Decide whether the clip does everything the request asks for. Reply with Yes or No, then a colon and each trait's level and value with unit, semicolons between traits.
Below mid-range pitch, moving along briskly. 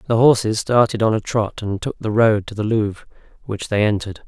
Yes: low, 110 Hz; fast, 225 wpm